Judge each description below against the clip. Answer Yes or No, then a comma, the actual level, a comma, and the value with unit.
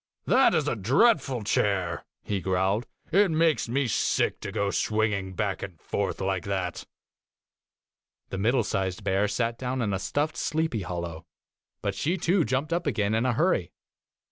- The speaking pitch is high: No, low, 105 Hz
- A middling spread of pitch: No, wide, 6.0 semitones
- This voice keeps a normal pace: Yes, average, 170 wpm